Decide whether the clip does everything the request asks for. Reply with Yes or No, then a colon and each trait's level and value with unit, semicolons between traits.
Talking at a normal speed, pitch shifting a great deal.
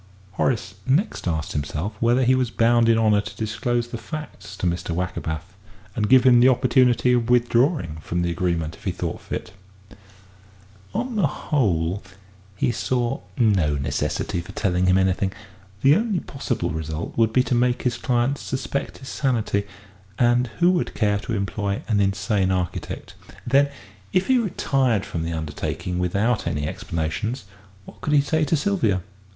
Yes: average, 165 wpm; wide, 6.1 semitones